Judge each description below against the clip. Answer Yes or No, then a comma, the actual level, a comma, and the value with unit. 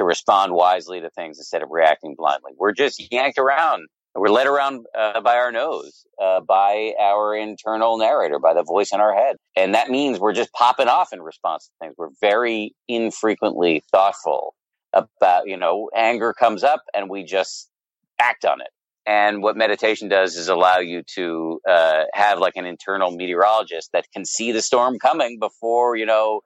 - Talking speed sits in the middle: Yes, average, 185 wpm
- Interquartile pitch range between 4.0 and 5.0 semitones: No, average, 2.9 semitones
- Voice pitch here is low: Yes, low, 110 Hz